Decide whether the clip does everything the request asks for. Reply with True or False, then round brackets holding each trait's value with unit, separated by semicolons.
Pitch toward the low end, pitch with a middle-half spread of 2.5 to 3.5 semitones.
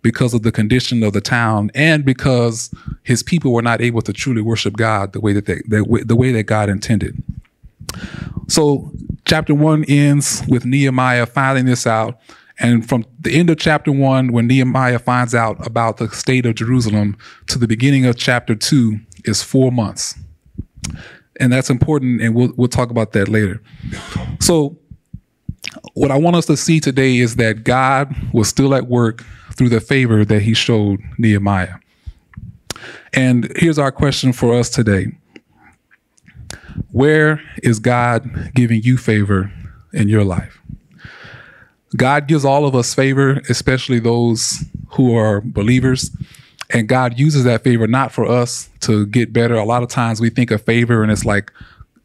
True (120 Hz; 3.2 semitones)